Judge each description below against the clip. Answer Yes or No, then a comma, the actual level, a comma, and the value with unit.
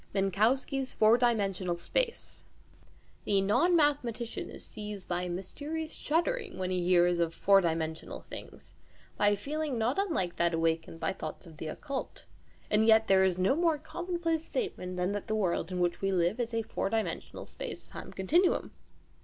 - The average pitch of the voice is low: No, high, 210 Hz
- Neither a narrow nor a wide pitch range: No, wide, 8.1 semitones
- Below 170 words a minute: No, average, 175 wpm